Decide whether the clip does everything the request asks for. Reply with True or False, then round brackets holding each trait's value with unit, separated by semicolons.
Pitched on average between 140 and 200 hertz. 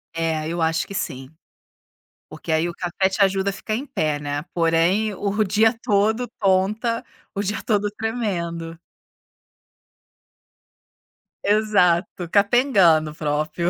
True (190 Hz)